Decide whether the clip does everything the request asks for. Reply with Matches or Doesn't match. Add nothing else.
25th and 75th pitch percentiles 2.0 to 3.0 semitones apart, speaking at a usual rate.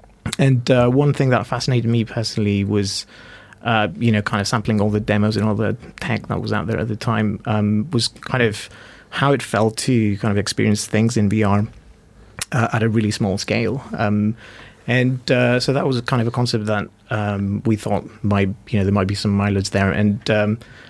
Doesn't match